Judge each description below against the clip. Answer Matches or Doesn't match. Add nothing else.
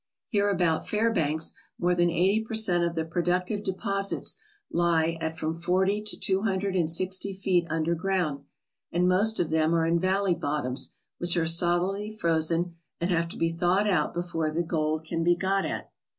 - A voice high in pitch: Doesn't match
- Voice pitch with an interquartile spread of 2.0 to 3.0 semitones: Matches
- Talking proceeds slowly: Doesn't match